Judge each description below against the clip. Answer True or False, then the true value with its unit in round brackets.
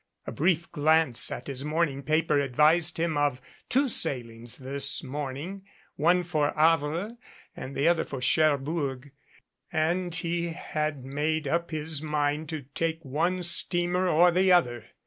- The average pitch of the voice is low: False (155 Hz)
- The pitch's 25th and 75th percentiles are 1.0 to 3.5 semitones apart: True (3.2 semitones)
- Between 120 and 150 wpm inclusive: True (145 wpm)